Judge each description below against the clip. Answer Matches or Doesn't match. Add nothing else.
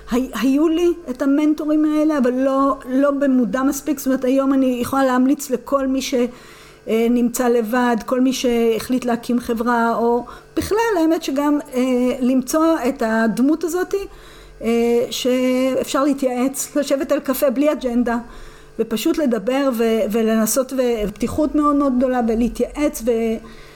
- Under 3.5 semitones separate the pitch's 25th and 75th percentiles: Matches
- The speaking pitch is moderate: Doesn't match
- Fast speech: Doesn't match